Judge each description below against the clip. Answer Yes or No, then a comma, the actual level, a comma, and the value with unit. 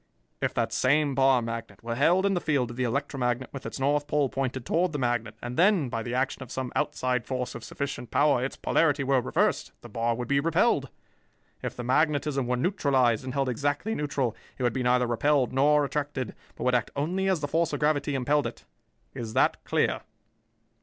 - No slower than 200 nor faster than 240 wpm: Yes, fast, 205 wpm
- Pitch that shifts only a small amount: No, average, 3.2 semitones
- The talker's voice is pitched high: No, low, 135 Hz